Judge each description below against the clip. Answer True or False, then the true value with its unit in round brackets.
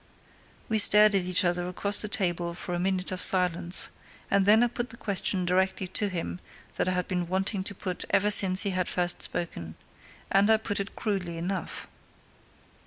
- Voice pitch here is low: False (185 Hz)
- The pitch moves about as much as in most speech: False (2.2 semitones)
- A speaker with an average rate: True (190 wpm)